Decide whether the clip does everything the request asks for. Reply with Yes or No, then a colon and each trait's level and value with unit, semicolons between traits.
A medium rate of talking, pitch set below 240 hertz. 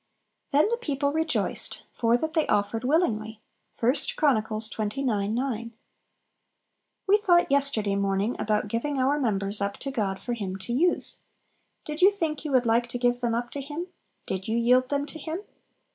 No: average, 175 wpm; high, 245 Hz